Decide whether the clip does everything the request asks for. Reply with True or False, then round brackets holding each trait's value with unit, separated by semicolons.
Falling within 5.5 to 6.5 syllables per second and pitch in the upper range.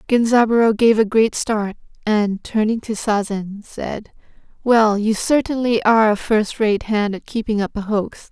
False (4.4 syllables/s; 215 Hz)